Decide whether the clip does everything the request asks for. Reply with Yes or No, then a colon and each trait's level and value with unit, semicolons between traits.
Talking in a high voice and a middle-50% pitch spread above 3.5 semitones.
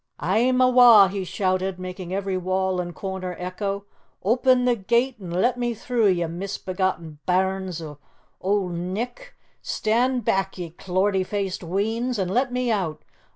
Yes: high, 195 Hz; average, 4.1 semitones